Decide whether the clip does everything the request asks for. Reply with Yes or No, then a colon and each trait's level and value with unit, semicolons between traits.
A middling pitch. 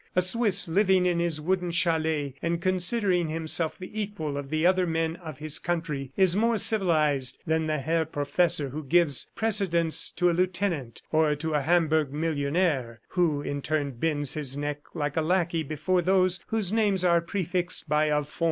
Yes: medium, 165 Hz